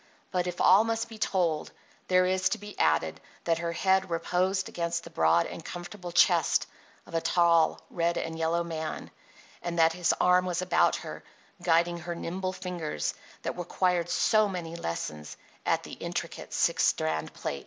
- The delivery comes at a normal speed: Yes, average, 170 wpm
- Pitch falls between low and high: Yes, medium, 175 Hz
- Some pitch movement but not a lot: No, narrow, 1.9 semitones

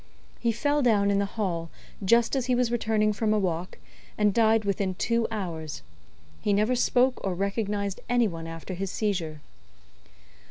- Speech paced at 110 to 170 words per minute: Yes, average, 165 wpm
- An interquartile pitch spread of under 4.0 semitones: Yes, average, 3.6 semitones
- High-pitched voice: Yes, high, 205 Hz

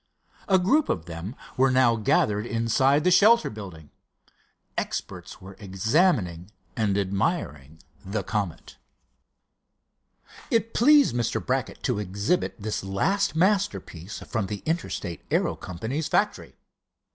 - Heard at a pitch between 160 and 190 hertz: No, low, 110 Hz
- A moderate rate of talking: No, slow, 115 wpm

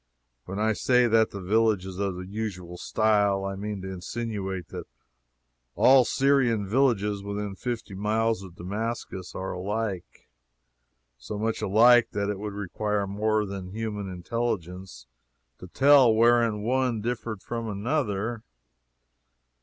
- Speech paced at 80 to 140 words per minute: Yes, slow, 135 wpm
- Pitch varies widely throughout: No, average, 2.9 semitones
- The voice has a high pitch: No, low, 105 Hz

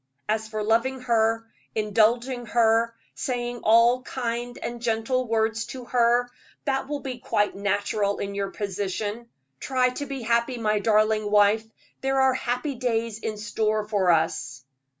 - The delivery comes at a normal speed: Yes, average, 150 wpm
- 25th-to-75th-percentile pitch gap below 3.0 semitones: Yes, narrow, 2.5 semitones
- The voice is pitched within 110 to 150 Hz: No, high, 230 Hz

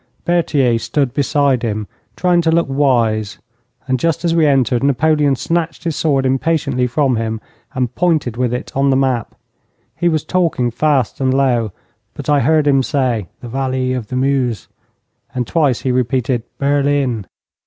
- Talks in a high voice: No, low, 135 Hz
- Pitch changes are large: No, average, 3.2 semitones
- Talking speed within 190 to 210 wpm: No, average, 165 wpm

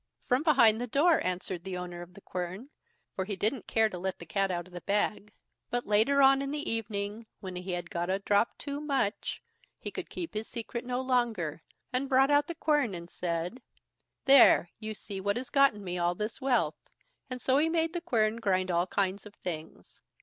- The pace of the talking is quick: Yes, fast, 210 wpm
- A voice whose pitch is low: No, high, 215 Hz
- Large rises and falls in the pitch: Yes, wide, 6.2 semitones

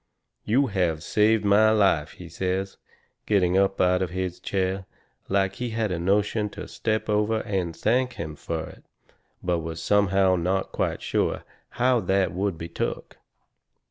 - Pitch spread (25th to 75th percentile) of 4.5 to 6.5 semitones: No, average, 2.8 semitones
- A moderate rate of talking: Yes, average, 160 wpm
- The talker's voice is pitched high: No, very low, 95 Hz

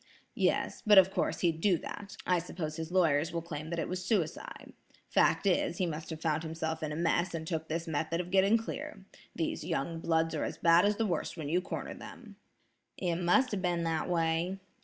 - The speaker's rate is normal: No, fast, 215 wpm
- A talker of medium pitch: Yes, medium, 170 Hz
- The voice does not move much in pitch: Yes, narrow, 2.3 semitones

